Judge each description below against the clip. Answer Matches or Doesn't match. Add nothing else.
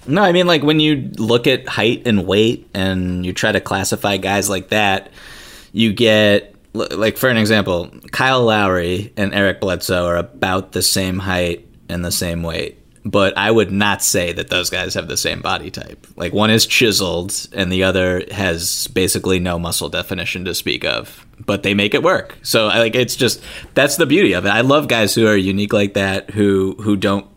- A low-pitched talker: Matches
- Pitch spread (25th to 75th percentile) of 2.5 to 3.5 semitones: Matches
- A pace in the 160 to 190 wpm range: Doesn't match